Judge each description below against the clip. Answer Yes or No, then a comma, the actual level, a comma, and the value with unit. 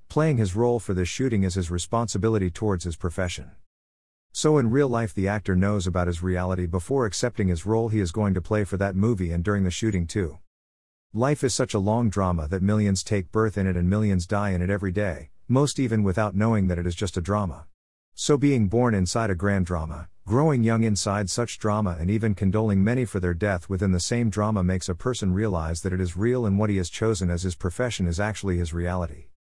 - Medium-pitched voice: No, low, 100 Hz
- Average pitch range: Yes, average, 3.5 semitones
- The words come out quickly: Yes, fast, 225 wpm